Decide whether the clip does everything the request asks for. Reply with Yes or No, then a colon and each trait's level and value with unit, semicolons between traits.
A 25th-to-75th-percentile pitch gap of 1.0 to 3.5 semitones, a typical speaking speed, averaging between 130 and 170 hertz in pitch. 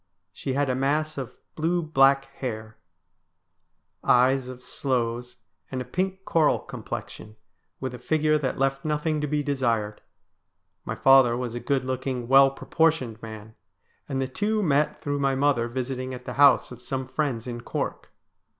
Yes: average, 2.9 semitones; average, 160 wpm; low, 135 Hz